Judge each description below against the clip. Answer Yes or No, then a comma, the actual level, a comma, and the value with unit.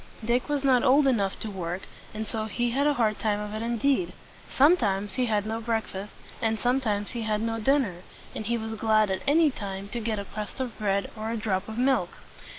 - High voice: Yes, high, 220 Hz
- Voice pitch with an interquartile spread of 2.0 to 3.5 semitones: Yes, average, 3.0 semitones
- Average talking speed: No, fast, 225 wpm